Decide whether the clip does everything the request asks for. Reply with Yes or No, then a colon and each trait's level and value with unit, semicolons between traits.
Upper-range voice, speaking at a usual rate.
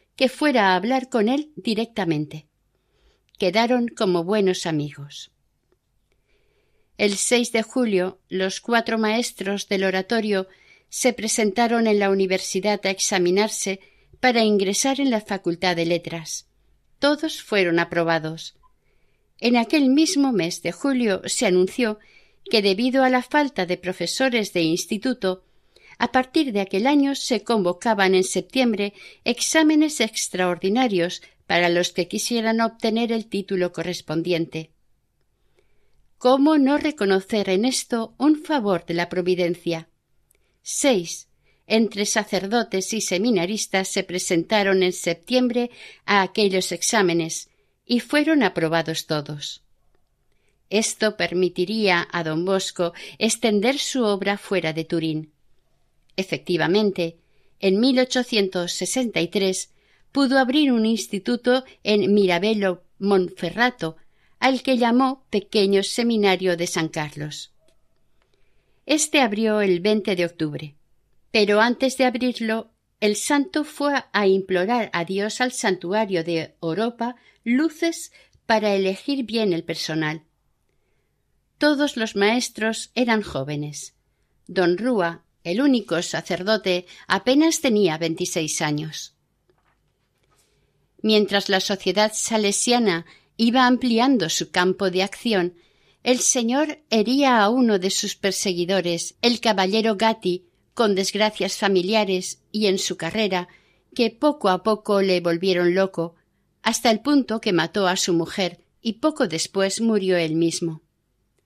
No: high, 200 Hz; slow, 115 wpm